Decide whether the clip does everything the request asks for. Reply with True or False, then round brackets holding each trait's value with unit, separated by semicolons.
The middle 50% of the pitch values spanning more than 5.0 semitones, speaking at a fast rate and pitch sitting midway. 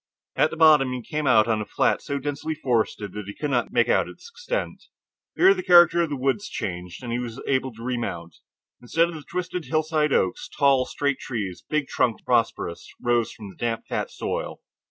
False (5.4 semitones; 210 wpm; 130 Hz)